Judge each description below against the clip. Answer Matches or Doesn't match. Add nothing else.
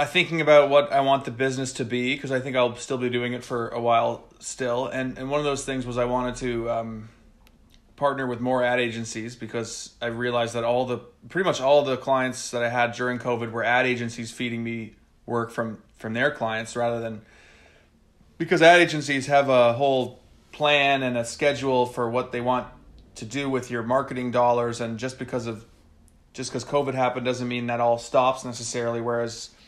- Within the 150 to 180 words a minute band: Doesn't match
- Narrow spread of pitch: Matches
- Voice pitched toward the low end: Matches